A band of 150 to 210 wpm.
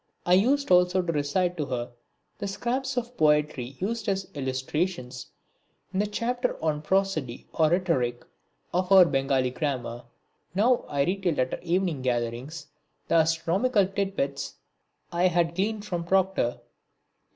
No: average, 140 wpm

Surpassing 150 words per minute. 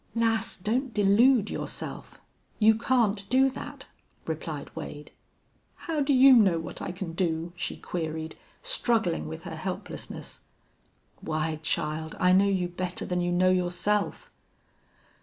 No: slow, 135 wpm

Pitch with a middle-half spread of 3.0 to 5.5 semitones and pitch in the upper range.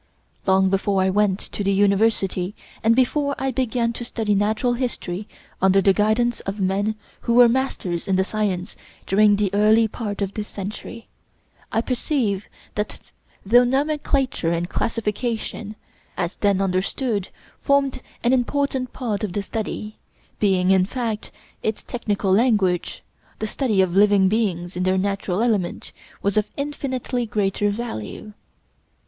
Yes: average, 3.6 semitones; high, 210 Hz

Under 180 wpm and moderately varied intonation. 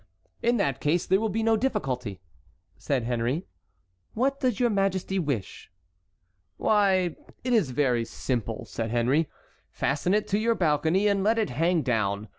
No: average, 155 wpm; wide, 8.9 semitones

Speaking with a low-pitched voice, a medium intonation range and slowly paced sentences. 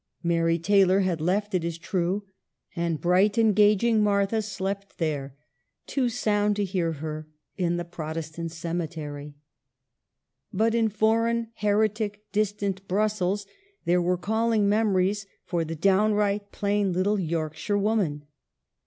No: high, 195 Hz; average, 3.6 semitones; slow, 125 wpm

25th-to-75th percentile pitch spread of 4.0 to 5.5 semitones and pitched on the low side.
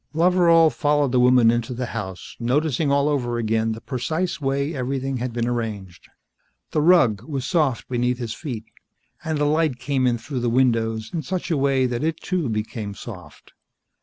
Yes: average, 4.3 semitones; low, 130 Hz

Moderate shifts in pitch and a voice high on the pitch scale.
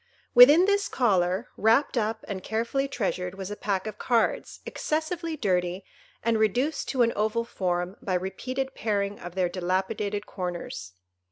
Yes: average, 4.9 semitones; high, 210 Hz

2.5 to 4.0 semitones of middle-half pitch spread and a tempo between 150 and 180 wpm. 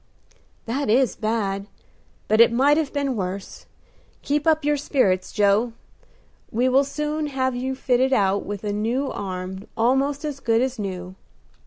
No: average, 5.3 semitones; average, 160 wpm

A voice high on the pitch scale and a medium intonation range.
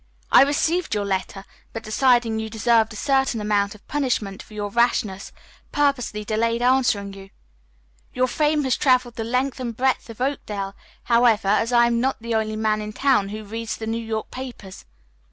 Yes: high, 230 Hz; average, 3.1 semitones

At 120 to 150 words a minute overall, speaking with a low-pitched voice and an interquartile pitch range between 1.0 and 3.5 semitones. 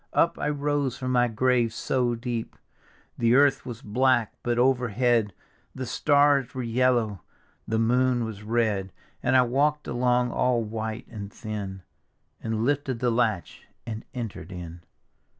Yes: average, 145 wpm; low, 120 Hz; narrow, 2.5 semitones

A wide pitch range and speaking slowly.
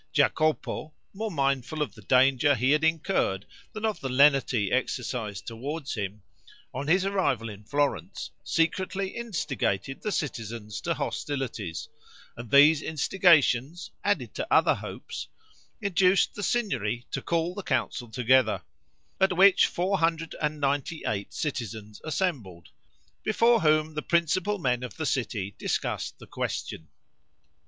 Yes: wide, 6.3 semitones; slow, 125 wpm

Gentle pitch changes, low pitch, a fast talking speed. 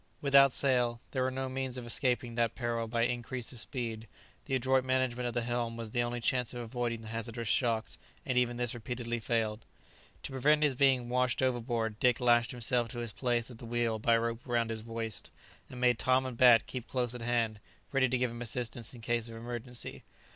Yes: narrow, 1.5 semitones; low, 120 Hz; fast, 215 wpm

